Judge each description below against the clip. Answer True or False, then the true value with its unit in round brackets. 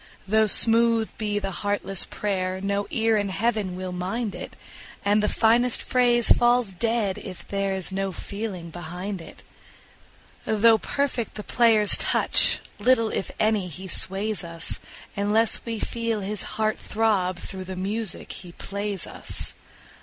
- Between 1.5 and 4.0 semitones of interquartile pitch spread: True (3.0 semitones)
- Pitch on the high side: True (205 Hz)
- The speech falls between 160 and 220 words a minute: False (145 wpm)